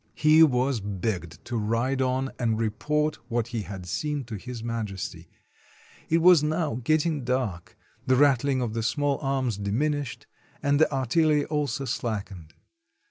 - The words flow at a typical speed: Yes, average, 150 wpm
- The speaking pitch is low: Yes, low, 130 Hz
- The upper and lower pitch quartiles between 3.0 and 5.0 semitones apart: Yes, average, 4.7 semitones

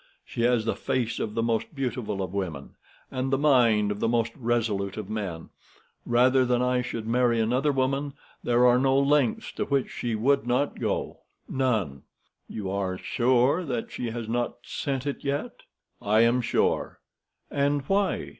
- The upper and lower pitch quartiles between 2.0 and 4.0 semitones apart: Yes, average, 3.3 semitones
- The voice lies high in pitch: No, low, 120 Hz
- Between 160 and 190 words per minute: Yes, average, 165 wpm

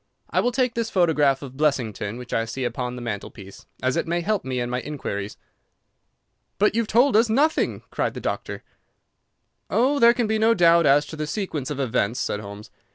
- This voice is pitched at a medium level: Yes, medium, 150 Hz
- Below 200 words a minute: No, fast, 205 wpm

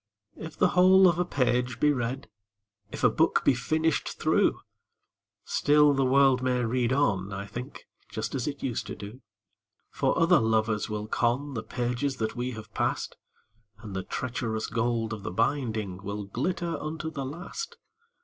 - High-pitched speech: No, low, 125 Hz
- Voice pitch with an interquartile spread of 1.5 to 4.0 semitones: No, average, 4.5 semitones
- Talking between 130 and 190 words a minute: Yes, average, 170 wpm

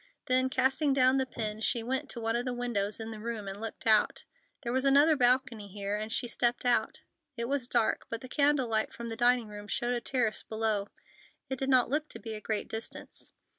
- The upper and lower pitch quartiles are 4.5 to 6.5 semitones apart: No, average, 2.9 semitones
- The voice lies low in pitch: No, high, 235 Hz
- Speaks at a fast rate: Yes, fast, 225 wpm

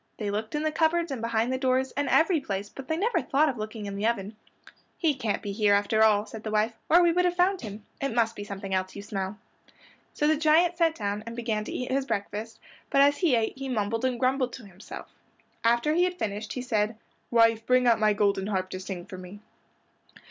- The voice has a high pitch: Yes, high, 230 Hz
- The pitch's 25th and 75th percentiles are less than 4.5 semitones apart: No, average, 5.1 semitones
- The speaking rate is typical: No, fast, 235 wpm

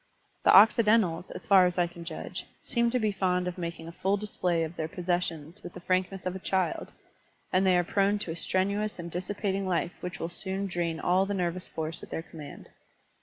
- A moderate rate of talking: No, fast, 215 wpm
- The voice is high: No, medium, 180 Hz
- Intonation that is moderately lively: No, narrow, 2.3 semitones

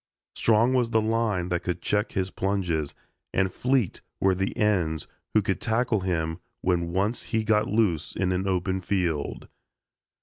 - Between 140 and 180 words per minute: Yes, average, 160 wpm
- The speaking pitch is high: No, very low, 95 Hz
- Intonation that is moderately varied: Yes, average, 3.5 semitones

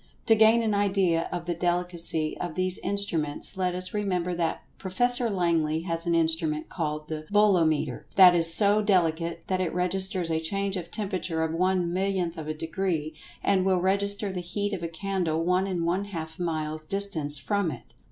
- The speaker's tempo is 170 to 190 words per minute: Yes, average, 180 wpm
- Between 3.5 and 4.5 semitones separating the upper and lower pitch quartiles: No, average, 3.1 semitones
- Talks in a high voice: No, medium, 180 Hz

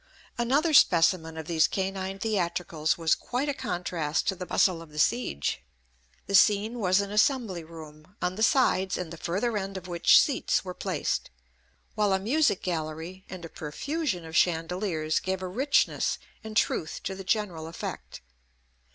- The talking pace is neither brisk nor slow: Yes, average, 165 wpm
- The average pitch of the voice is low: No, medium, 185 Hz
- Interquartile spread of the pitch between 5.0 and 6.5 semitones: No, average, 4.2 semitones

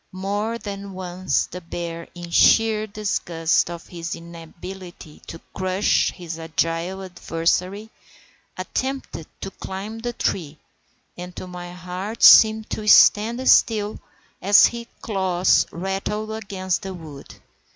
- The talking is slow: Yes, slow, 120 wpm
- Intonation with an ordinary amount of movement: Yes, average, 3.6 semitones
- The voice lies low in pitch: No, medium, 185 Hz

